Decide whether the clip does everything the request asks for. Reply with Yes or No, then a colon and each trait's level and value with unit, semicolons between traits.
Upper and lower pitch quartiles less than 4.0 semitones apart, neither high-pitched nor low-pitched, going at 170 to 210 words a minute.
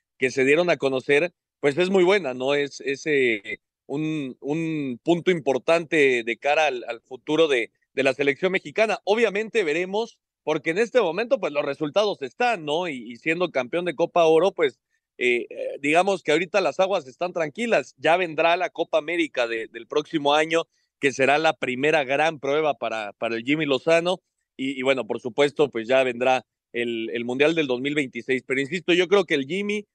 No: average, 5.1 semitones; medium, 155 Hz; fast, 190 wpm